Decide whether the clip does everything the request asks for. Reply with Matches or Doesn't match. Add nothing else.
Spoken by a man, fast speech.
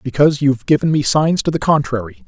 Matches